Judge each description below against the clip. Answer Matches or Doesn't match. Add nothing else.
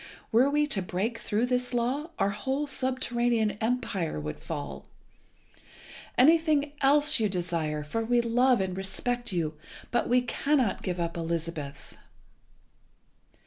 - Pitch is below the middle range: Doesn't match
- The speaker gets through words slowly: Matches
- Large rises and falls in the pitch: Matches